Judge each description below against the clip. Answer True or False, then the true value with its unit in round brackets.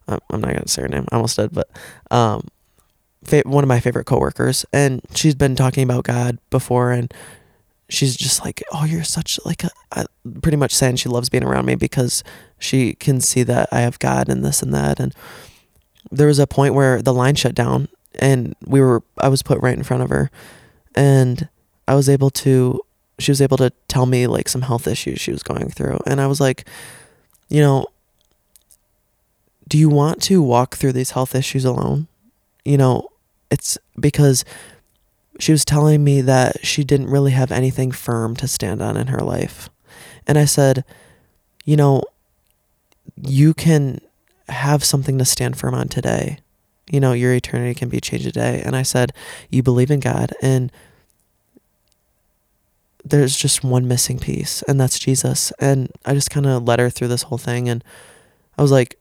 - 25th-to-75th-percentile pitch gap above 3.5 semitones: False (2.4 semitones)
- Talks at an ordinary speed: True (185 wpm)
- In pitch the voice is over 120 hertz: True (130 Hz)